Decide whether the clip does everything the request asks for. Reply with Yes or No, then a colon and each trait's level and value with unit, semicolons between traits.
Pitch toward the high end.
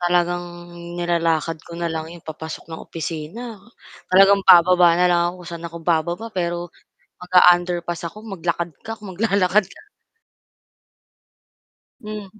No: medium, 175 Hz